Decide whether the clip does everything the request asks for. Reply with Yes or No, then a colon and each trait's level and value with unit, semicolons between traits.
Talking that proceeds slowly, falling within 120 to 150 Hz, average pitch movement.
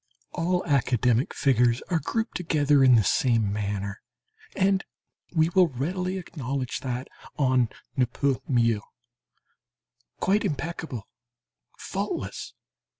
No: slow, 105 wpm; low, 135 Hz; wide, 5.8 semitones